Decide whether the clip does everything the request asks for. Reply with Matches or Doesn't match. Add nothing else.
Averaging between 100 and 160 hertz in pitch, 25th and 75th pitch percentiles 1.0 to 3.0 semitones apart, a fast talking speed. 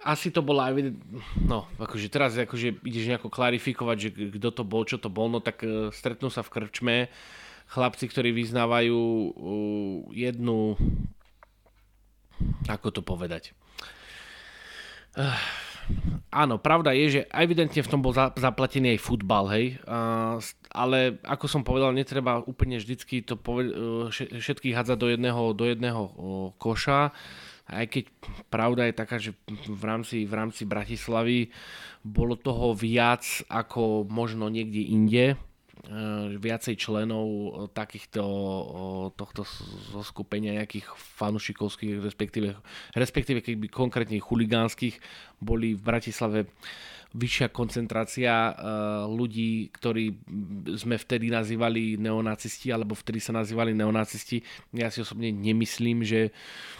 Doesn't match